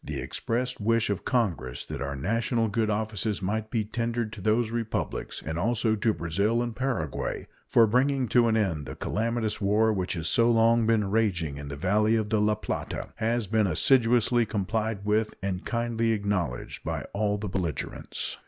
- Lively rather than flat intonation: No, average, 2.7 semitones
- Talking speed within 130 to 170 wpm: No, average, 180 wpm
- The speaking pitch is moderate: No, low, 110 Hz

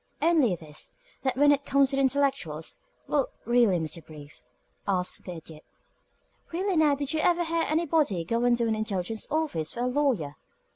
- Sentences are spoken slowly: No, average, 180 wpm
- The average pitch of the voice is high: Yes, high, 245 Hz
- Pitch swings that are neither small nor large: No, wide, 8.6 semitones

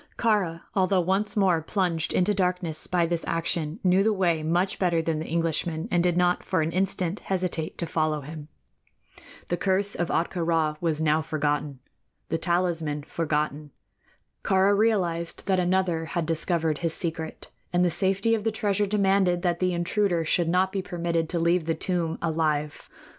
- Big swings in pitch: No, narrow, 2.6 semitones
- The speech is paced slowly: No, average, 170 wpm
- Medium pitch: Yes, medium, 170 Hz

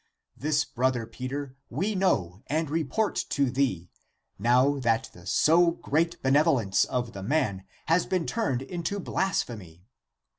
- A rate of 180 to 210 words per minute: No, average, 140 wpm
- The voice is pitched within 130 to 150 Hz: Yes, low, 135 Hz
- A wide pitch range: Yes, wide, 6.0 semitones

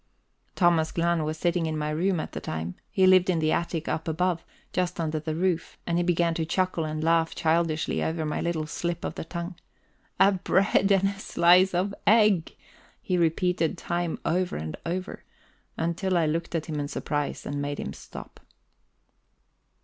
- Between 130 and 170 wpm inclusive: No, average, 180 wpm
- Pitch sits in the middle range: Yes, medium, 170 Hz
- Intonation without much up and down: Yes, narrow, 2.3 semitones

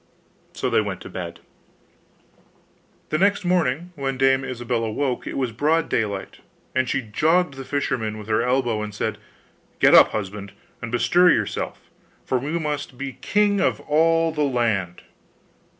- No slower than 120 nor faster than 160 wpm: Yes, average, 155 wpm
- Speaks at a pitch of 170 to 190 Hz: No, low, 130 Hz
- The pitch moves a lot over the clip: Yes, wide, 5.8 semitones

